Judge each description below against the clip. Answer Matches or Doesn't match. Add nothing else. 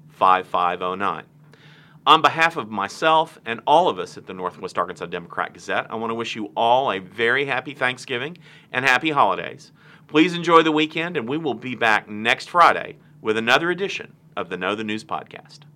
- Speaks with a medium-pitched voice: Matches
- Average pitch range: Doesn't match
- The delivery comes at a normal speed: Matches